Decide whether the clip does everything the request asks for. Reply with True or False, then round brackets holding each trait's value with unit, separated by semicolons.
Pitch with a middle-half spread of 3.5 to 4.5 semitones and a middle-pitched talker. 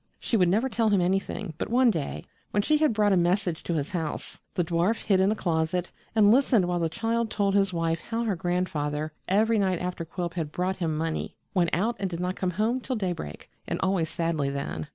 True (4.0 semitones; 180 Hz)